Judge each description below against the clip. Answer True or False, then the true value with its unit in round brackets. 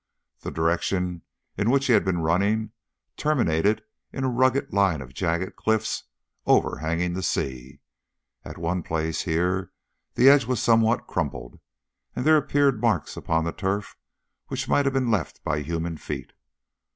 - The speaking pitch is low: True (95 Hz)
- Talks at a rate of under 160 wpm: True (150 wpm)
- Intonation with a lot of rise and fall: True (6.4 semitones)